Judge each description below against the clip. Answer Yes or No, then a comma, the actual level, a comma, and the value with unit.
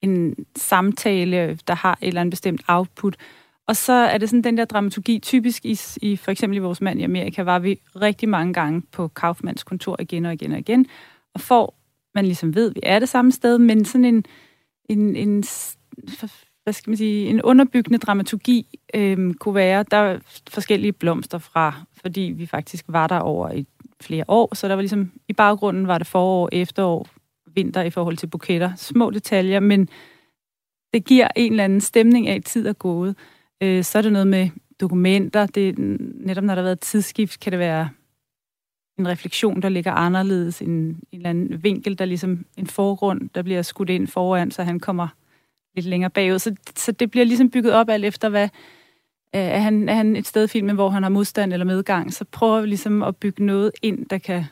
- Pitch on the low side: No, high, 195 Hz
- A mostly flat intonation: No, average, 3.2 semitones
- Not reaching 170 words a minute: No, average, 200 wpm